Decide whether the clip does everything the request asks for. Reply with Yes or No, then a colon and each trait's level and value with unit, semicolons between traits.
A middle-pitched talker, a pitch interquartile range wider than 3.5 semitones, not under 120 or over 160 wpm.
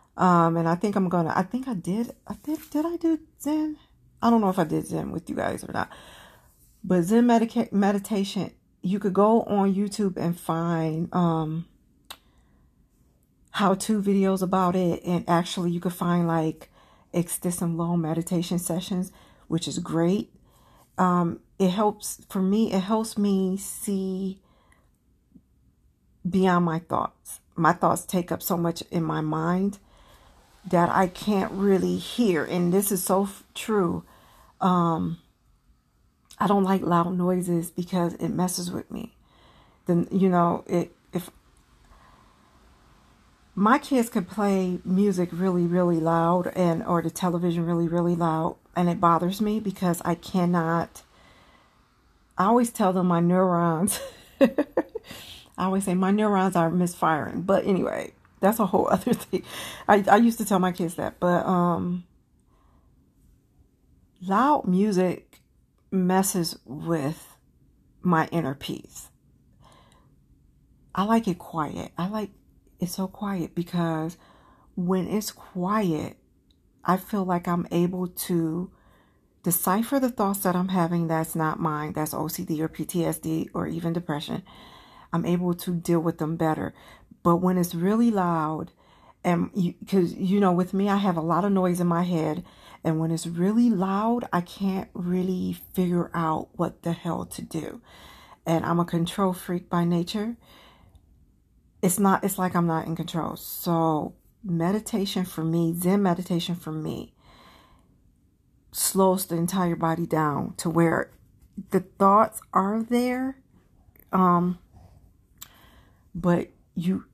No: medium, 180 Hz; narrow, 2.6 semitones; average, 145 wpm